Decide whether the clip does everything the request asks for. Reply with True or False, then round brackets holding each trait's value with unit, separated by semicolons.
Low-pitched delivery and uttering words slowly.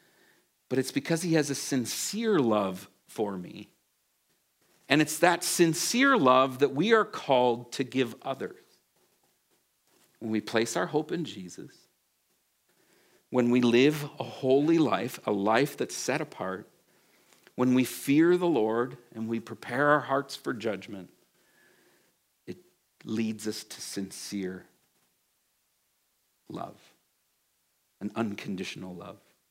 True (130 Hz; 125 wpm)